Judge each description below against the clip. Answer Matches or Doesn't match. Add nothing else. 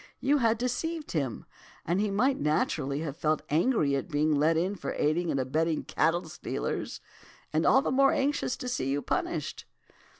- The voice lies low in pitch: Doesn't match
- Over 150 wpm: Matches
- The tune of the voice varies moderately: Doesn't match